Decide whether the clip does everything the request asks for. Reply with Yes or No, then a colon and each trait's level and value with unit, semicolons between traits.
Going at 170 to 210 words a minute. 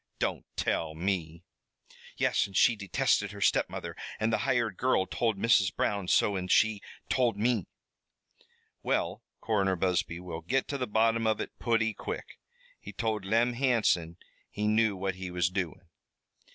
No: average, 155 wpm